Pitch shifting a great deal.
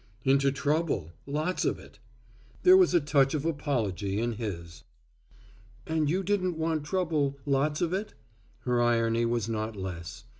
Yes: wide, 5.9 semitones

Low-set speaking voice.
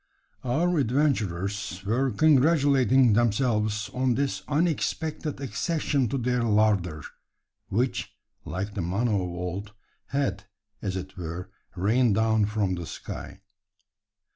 Yes: low, 110 Hz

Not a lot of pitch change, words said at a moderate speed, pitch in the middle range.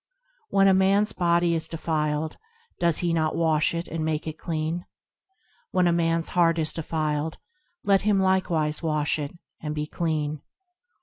Yes: narrow, 2.0 semitones; average, 160 wpm; medium, 165 Hz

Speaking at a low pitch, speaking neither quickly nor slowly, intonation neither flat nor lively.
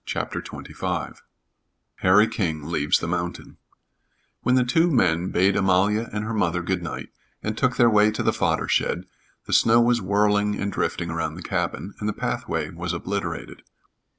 Yes: low, 100 Hz; average, 170 wpm; average, 3.8 semitones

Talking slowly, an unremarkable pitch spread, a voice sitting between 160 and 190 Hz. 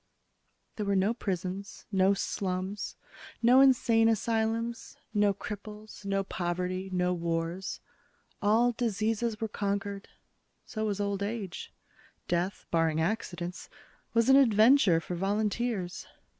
No: slow, 115 wpm; average, 3.2 semitones; high, 200 Hz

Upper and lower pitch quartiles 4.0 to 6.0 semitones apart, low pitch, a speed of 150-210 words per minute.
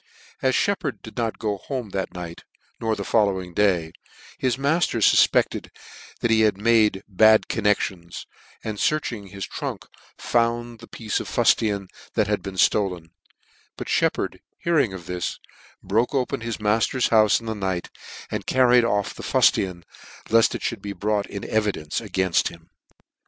No: average, 3.4 semitones; low, 105 Hz; average, 160 wpm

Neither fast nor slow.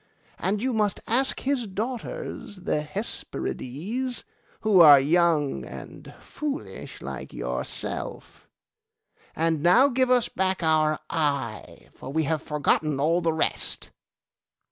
No: slow, 120 wpm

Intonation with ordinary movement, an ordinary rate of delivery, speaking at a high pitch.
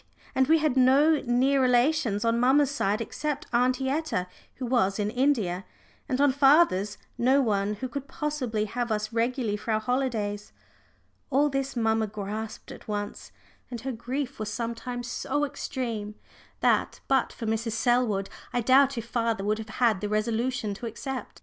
Yes: average, 3.7 semitones; average, 165 wpm; high, 240 Hz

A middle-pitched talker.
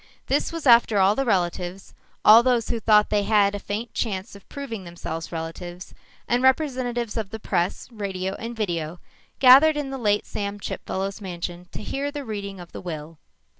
No: high, 205 Hz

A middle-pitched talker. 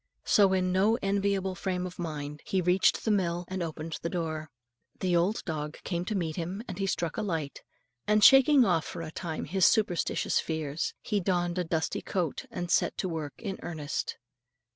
Yes: medium, 180 Hz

